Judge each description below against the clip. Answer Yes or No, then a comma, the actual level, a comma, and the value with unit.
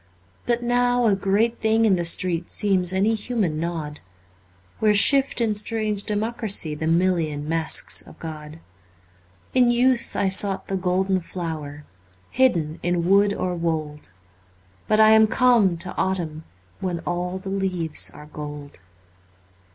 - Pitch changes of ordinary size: Yes, average, 4.7 semitones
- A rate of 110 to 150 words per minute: Yes, average, 140 wpm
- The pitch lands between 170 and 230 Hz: Yes, high, 190 Hz